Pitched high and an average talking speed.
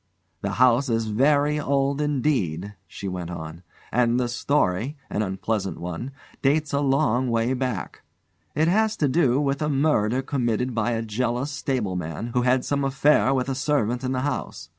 No: low, 125 Hz; average, 170 wpm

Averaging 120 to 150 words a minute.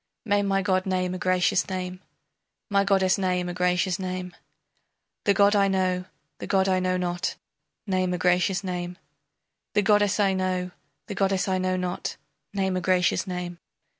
No: average, 165 wpm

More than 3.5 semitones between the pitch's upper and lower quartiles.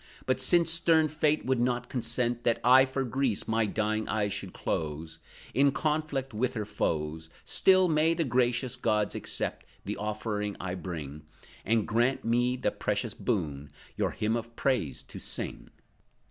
Yes: average, 4.3 semitones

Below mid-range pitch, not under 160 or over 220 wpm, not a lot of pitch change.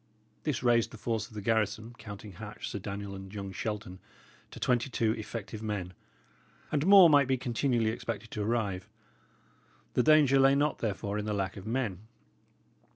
No: low, 110 Hz; average, 170 wpm; average, 3.4 semitones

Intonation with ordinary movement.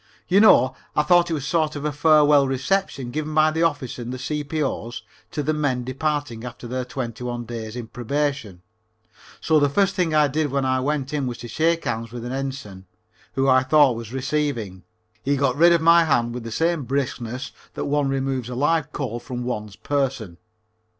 Yes: average, 3.7 semitones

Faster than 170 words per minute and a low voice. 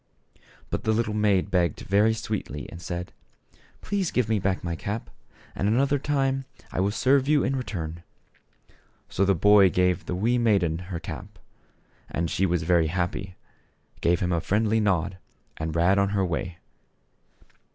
No: average, 165 wpm; very low, 95 Hz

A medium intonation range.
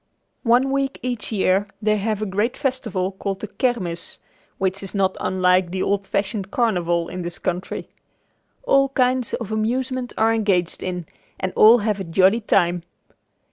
Yes: average, 4.2 semitones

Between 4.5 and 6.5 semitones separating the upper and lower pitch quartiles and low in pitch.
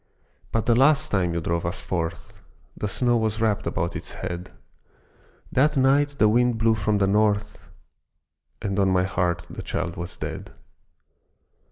Yes: average, 5.0 semitones; low, 105 Hz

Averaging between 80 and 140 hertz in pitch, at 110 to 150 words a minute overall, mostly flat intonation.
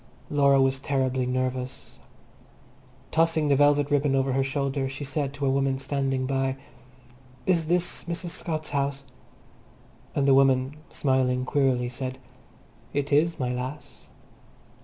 Yes: low, 135 Hz; slow, 135 wpm; narrow, 1.7 semitones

